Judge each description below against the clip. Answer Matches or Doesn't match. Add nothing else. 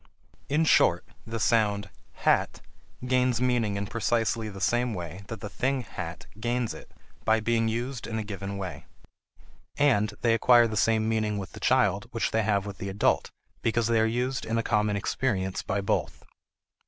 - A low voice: Matches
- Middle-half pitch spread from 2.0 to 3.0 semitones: Matches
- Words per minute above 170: Matches